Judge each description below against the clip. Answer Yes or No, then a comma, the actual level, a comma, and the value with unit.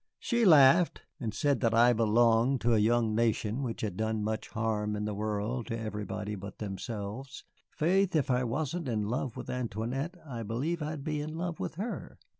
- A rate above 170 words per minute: Yes, average, 190 wpm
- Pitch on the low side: Yes, low, 115 Hz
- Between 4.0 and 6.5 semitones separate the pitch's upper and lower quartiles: Yes, average, 4.7 semitones